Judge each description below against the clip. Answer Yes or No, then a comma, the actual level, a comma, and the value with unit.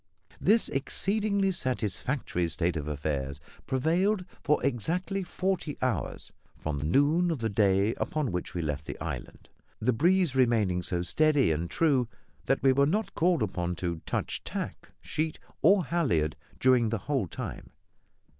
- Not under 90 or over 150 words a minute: Yes, average, 145 wpm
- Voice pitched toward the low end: Yes, low, 130 Hz